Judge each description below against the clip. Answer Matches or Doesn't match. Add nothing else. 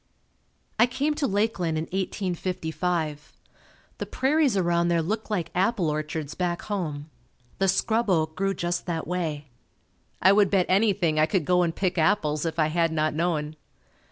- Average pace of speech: Matches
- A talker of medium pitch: Matches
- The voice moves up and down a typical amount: Matches